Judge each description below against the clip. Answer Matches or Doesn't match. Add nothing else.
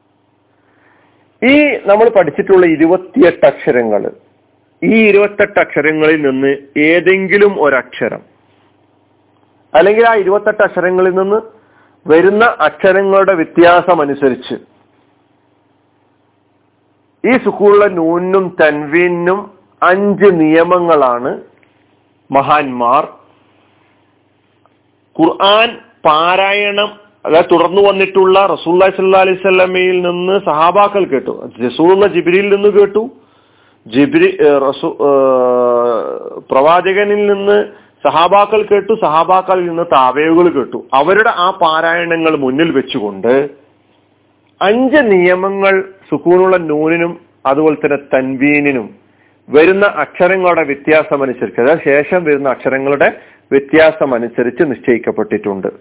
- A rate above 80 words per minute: Doesn't match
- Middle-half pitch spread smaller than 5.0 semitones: Doesn't match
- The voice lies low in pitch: Doesn't match